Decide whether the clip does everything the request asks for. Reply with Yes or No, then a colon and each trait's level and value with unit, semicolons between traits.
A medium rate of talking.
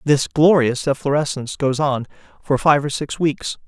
Yes: average, 165 wpm